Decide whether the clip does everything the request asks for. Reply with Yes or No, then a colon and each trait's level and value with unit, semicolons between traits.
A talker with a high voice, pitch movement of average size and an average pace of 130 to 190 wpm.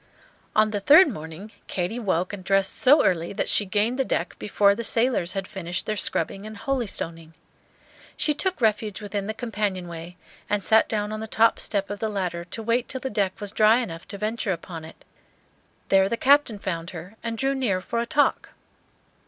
No: high, 205 Hz; average, 3.7 semitones; average, 200 wpm